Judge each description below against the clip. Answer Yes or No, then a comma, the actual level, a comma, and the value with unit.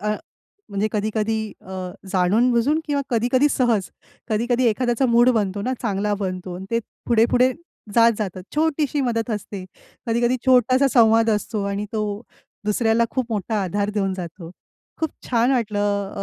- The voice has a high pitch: Yes, high, 225 Hz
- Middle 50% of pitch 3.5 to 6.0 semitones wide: No, average, 3.1 semitones